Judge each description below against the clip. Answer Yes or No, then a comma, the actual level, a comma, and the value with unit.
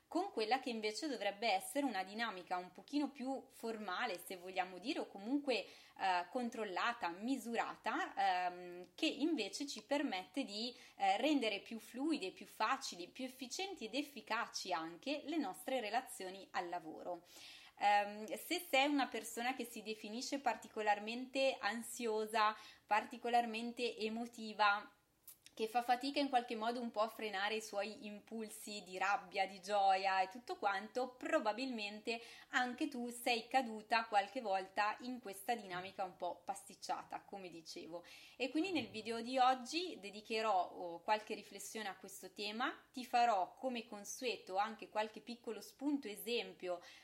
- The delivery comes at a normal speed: Yes, average, 140 wpm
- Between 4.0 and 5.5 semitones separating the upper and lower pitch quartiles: Yes, average, 4.4 semitones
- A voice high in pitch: Yes, high, 225 Hz